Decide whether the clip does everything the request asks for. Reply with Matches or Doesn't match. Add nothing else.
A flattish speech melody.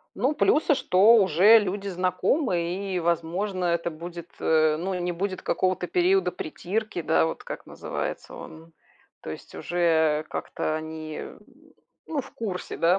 Doesn't match